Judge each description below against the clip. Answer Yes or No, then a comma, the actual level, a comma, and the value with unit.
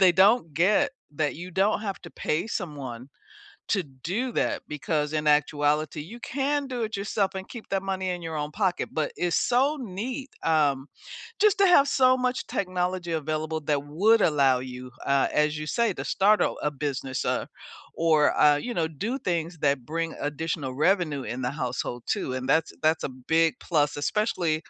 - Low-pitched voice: No, medium, 165 Hz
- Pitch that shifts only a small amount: No, wide, 5.5 semitones